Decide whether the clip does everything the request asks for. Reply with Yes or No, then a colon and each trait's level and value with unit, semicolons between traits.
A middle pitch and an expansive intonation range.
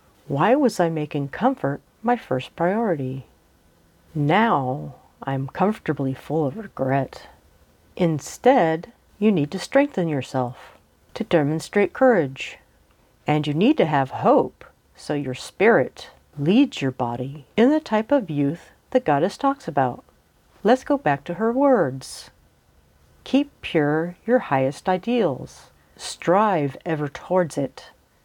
Yes: medium, 155 Hz; wide, 8.5 semitones